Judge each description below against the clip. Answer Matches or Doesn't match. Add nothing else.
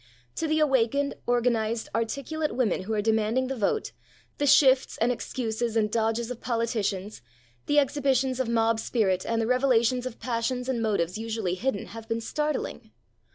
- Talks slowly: Doesn't match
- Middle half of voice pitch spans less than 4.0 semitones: Matches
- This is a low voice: Doesn't match